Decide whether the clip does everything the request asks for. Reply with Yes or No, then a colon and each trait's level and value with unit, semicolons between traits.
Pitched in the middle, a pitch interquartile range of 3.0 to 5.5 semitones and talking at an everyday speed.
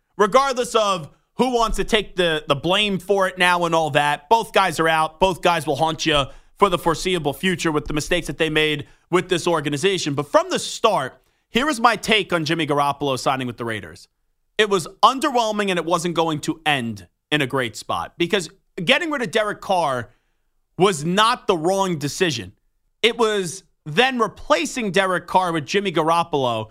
Yes: medium, 175 Hz; average, 5.1 semitones; average, 190 wpm